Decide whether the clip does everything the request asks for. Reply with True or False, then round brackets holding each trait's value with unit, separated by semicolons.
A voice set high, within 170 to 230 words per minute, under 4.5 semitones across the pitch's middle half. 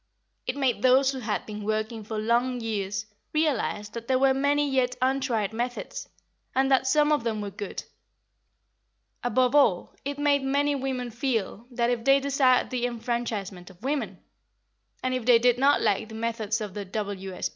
True (245 Hz; 175 wpm; 3.7 semitones)